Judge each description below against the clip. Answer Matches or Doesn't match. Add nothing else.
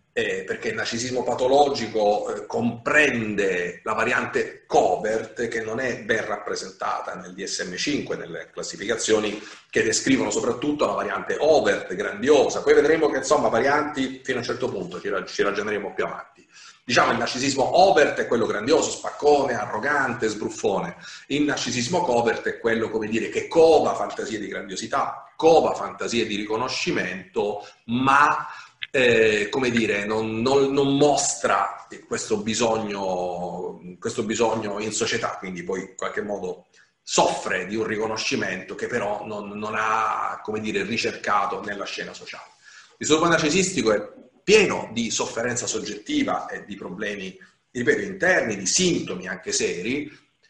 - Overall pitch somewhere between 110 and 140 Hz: Matches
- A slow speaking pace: Doesn't match